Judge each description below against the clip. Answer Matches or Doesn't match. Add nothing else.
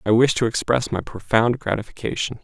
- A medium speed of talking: Matches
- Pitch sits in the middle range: Doesn't match